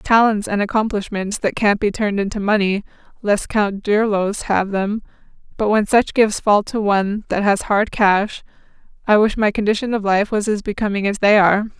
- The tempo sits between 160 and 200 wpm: Yes, average, 190 wpm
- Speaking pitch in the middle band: No, high, 205 Hz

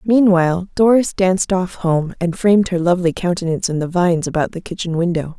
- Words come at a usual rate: Yes, average, 190 wpm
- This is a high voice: No, medium, 180 Hz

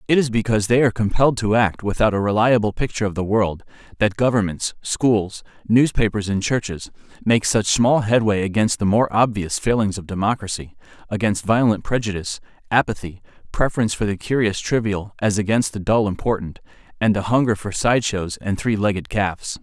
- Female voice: No, male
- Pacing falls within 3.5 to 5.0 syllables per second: No, 5.7 syllables/s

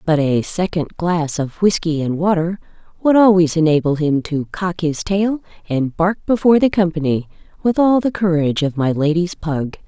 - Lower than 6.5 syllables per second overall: Yes, 5.0 syllables/s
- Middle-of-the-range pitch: Yes, medium, 175 Hz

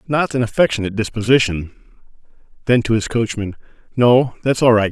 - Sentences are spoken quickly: No, average, 145 wpm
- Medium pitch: No, low, 115 Hz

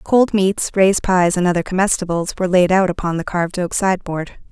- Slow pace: No, average, 200 wpm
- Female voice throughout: Yes, female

